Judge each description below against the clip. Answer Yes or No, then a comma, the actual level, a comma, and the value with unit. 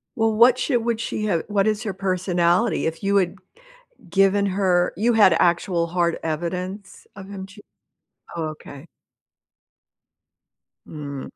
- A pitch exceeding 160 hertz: Yes, high, 190 Hz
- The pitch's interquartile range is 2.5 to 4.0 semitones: Yes, average, 3.3 semitones